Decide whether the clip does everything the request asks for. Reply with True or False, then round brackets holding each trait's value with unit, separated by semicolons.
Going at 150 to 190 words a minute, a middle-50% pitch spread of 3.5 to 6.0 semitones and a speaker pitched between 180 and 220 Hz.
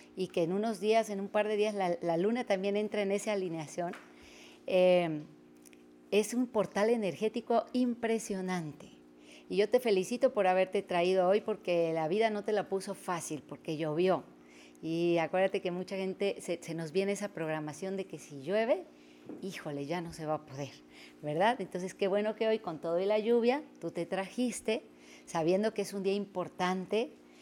True (185 wpm; 4.4 semitones; 185 Hz)